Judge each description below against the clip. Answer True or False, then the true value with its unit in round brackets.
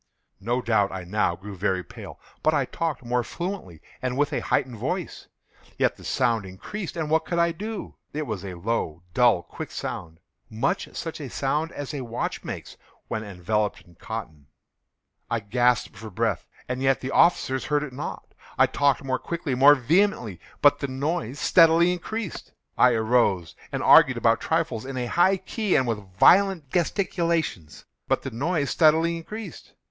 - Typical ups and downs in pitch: False (7.1 semitones)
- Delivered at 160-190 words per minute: True (165 wpm)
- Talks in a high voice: False (130 Hz)